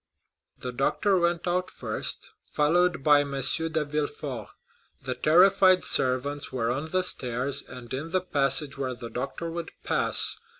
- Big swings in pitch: No, average, 4.8 semitones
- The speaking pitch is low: No, medium, 145 Hz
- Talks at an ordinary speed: Yes, average, 145 wpm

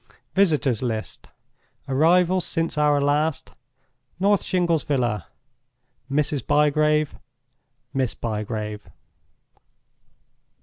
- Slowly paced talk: Yes, slow, 60 wpm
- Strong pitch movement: No, average, 4.1 semitones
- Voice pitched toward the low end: No, medium, 145 Hz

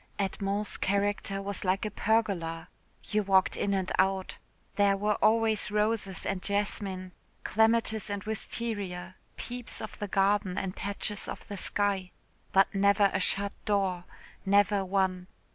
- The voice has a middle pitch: No, high, 200 Hz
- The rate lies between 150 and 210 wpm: No, average, 140 wpm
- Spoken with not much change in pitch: Yes, narrow, 1.6 semitones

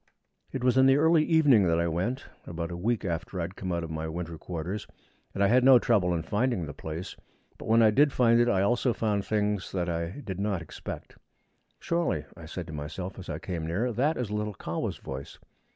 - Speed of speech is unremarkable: No, fast, 225 wpm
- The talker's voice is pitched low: Yes, low, 100 Hz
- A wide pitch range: Yes, wide, 6.0 semitones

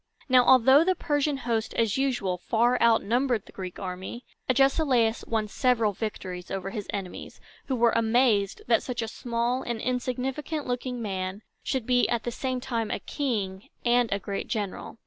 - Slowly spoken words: No, average, 165 wpm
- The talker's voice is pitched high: Yes, high, 235 Hz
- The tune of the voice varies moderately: Yes, average, 3.5 semitones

